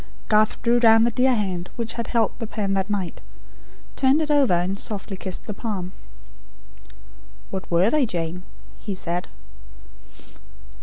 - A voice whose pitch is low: No, high, 210 Hz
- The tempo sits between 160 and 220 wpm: No, average, 150 wpm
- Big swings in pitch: No, average, 4.1 semitones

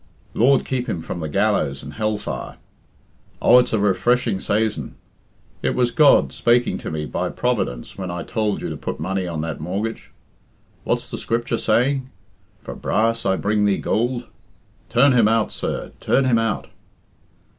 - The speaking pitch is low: Yes, low, 110 Hz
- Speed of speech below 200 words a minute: Yes, average, 165 wpm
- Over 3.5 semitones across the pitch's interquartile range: Yes, average, 4.3 semitones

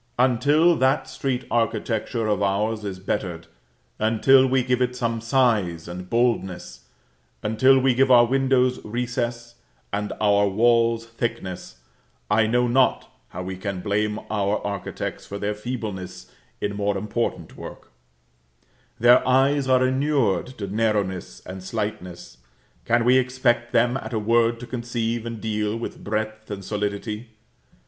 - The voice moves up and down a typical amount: Yes, average, 3.3 semitones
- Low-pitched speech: Yes, low, 115 Hz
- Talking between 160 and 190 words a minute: No, average, 140 wpm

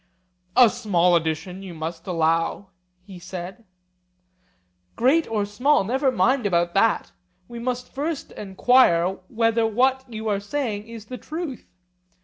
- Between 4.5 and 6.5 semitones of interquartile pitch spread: Yes, wide, 5.5 semitones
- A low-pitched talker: No, high, 215 Hz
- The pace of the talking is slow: Yes, slow, 130 wpm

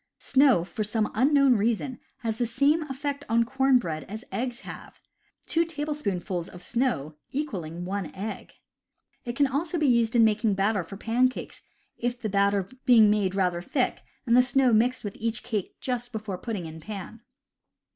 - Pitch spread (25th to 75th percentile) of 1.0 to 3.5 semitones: No, average, 4.4 semitones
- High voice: Yes, high, 230 Hz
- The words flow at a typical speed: Yes, average, 170 wpm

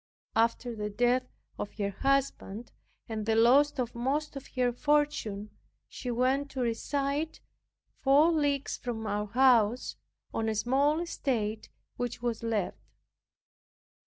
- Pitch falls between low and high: No, high, 245 Hz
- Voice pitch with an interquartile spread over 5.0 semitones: No, average, 3.8 semitones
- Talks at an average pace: No, slow, 130 wpm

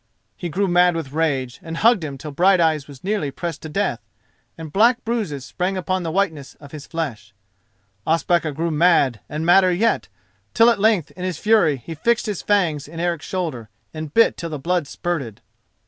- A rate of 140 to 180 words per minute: No, average, 190 wpm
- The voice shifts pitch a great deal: No, average, 4.0 semitones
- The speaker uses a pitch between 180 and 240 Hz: No, medium, 165 Hz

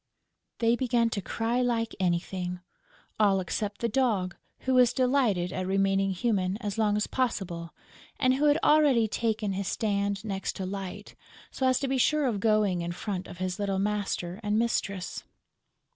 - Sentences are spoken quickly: No, average, 170 wpm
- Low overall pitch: No, high, 205 Hz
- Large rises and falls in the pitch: No, average, 3.7 semitones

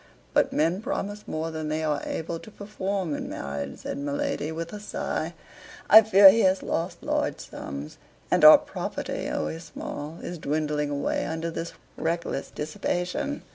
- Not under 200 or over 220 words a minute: No, average, 165 wpm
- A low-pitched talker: No, medium, 165 Hz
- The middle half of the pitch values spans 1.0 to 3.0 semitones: No, average, 4.0 semitones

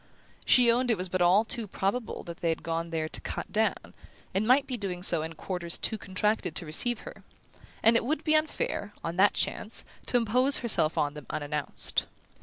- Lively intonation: Yes, wide, 6.3 semitones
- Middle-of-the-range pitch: No, high, 200 Hz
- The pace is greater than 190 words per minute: Yes, average, 200 wpm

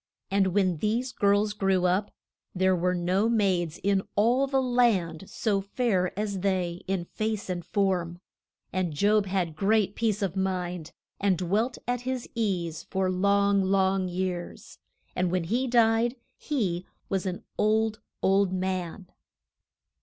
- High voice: Yes, high, 195 Hz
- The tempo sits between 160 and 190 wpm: No, average, 145 wpm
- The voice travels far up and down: No, average, 2.8 semitones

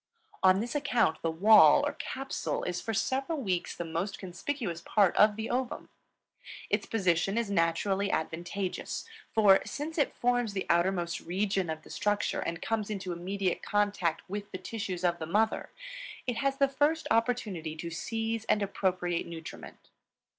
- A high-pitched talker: Yes, high, 200 Hz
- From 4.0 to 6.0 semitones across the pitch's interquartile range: Yes, average, 4.5 semitones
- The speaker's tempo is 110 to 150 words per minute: No, average, 160 wpm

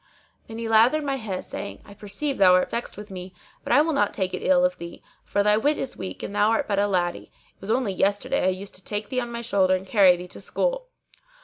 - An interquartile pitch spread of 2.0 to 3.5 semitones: No, average, 4.7 semitones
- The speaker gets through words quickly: Yes, fast, 260 wpm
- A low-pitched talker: No, high, 205 Hz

